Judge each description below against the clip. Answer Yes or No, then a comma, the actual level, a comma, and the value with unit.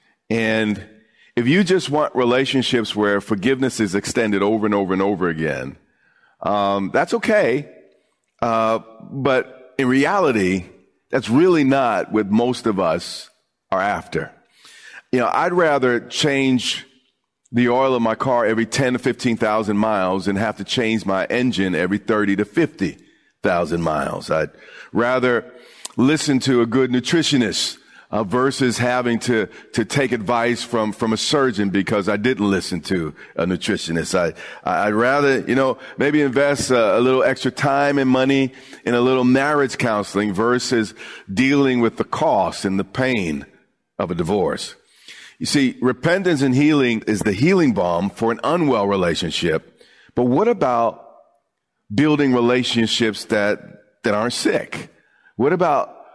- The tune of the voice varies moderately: Yes, average, 3.8 semitones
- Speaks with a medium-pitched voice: No, low, 120 Hz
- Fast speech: No, average, 150 wpm